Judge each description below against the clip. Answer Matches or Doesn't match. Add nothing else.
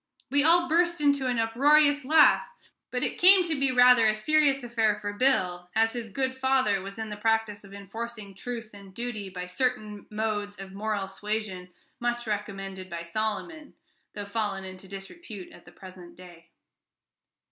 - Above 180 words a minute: Doesn't match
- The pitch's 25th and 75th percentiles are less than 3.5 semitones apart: Doesn't match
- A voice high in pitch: Matches